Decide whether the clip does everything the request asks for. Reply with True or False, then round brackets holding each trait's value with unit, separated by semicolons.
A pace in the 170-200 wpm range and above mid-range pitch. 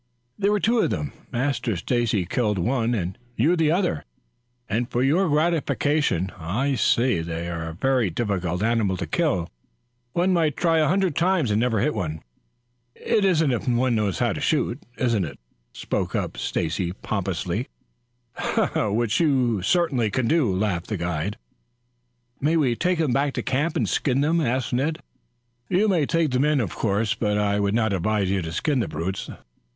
False (175 wpm; 120 Hz)